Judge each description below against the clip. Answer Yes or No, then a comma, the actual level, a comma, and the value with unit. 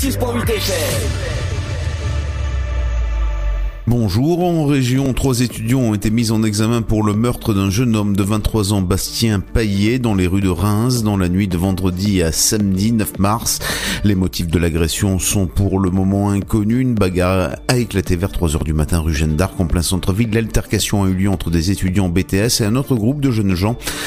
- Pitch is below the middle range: Yes, low, 100 Hz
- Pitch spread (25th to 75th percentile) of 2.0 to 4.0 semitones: Yes, average, 3.5 semitones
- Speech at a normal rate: Yes, average, 180 wpm